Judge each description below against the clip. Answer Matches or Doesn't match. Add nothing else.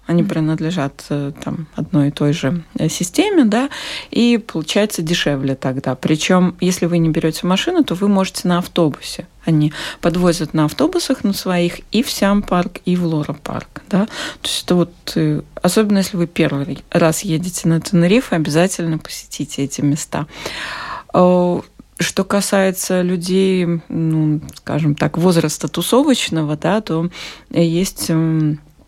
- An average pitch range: Matches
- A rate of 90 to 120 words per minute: Doesn't match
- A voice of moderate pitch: Matches